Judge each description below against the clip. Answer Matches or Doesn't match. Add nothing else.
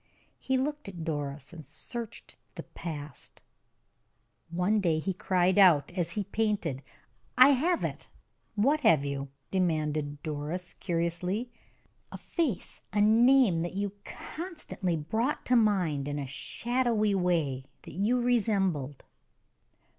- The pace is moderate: Doesn't match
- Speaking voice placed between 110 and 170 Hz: Doesn't match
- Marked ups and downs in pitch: Matches